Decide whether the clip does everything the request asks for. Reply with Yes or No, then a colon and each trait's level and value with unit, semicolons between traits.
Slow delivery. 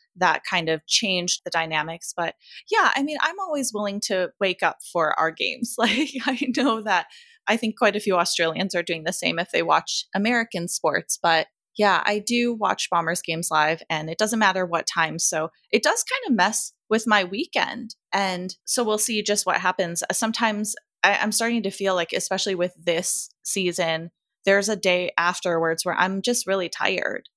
No: average, 195 wpm